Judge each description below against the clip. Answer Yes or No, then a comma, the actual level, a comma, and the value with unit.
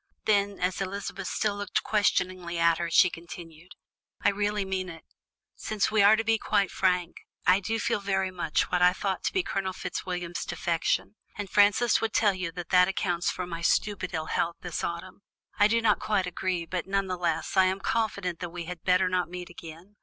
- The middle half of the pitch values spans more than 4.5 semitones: No, narrow, 2.4 semitones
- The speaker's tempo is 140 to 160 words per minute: No, fast, 205 wpm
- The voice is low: No, medium, 185 Hz